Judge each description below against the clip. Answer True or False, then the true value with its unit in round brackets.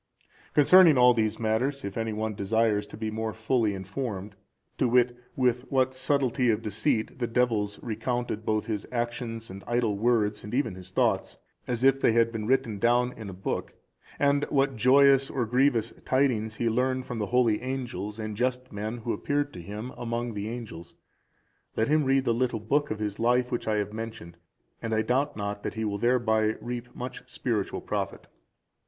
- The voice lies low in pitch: True (115 Hz)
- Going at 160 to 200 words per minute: True (185 wpm)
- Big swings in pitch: False (2.9 semitones)